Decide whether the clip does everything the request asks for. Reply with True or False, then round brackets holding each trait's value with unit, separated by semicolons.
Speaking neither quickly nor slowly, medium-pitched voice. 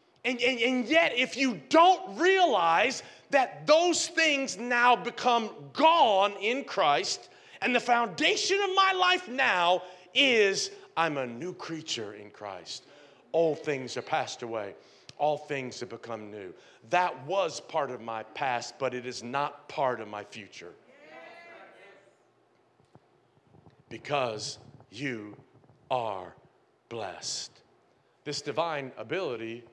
False (125 wpm; 180 Hz)